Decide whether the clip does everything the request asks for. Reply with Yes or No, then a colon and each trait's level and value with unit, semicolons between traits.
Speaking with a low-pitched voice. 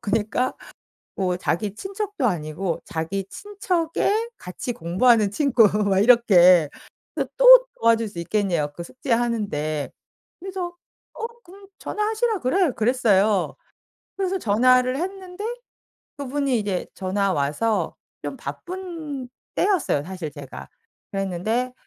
No: high, 230 Hz